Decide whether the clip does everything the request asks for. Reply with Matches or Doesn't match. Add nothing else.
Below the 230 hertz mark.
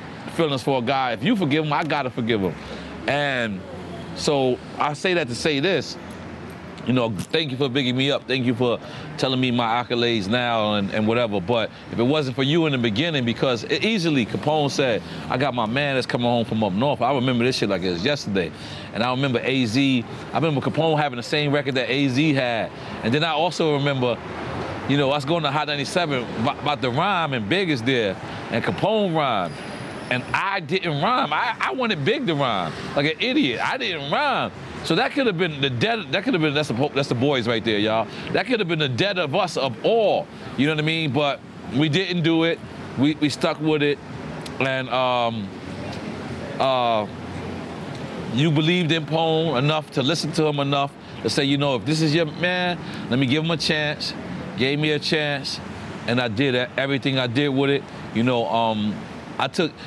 Matches